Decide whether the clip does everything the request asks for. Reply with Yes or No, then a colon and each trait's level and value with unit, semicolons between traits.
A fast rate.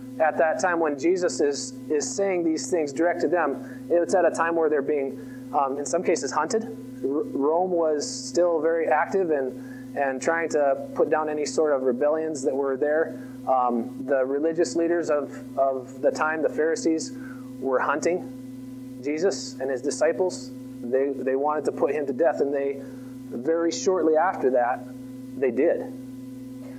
No: average, 170 wpm